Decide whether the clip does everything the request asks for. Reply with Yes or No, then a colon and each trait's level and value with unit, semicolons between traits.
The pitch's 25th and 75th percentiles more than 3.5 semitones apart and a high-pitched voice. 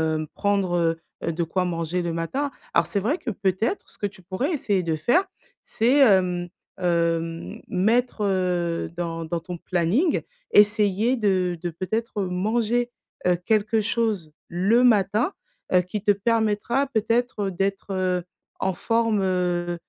Yes: average, 4.2 semitones; high, 195 Hz